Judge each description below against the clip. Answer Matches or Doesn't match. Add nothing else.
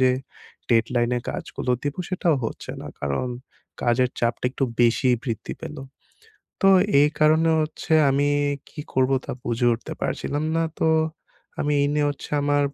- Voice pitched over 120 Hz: Matches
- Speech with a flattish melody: Doesn't match